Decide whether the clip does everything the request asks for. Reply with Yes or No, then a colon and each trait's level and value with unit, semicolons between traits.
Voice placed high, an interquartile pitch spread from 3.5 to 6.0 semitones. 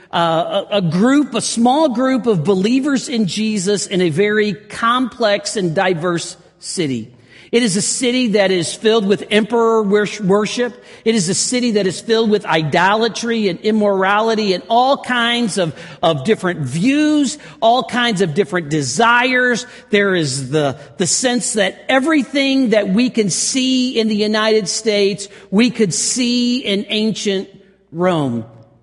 Yes: high, 210 Hz; average, 4.0 semitones